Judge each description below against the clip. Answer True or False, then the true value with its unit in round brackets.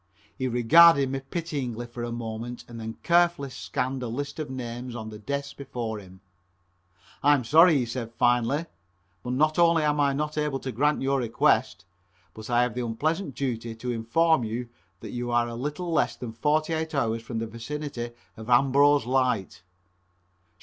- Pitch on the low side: True (125 Hz)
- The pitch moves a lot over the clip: False (4.0 semitones)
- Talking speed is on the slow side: False (180 wpm)